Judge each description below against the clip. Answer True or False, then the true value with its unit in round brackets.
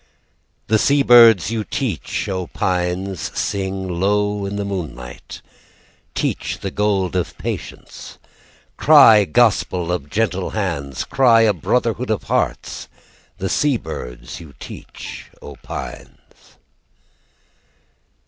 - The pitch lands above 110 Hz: False (95 Hz)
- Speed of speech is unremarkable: False (110 wpm)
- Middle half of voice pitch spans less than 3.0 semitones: False (3.5 semitones)